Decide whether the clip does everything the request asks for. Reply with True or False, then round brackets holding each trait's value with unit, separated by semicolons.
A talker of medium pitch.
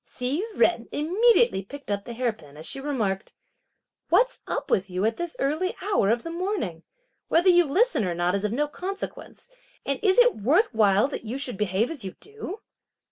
False (270 Hz)